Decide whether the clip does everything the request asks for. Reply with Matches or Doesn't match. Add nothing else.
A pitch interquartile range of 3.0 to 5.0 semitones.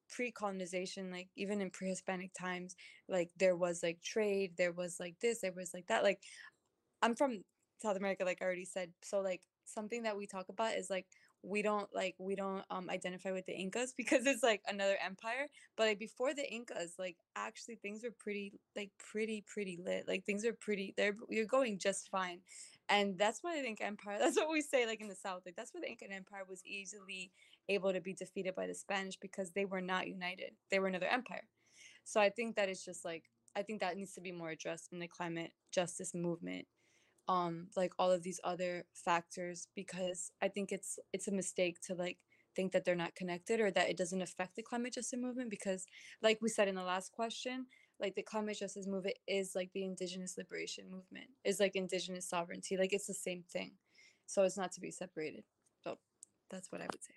Doesn't match